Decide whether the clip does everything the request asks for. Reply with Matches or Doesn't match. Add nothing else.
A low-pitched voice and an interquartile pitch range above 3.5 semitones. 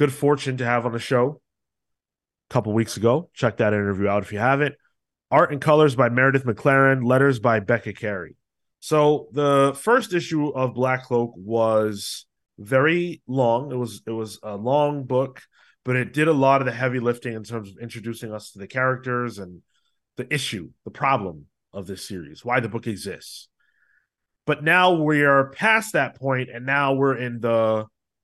Matches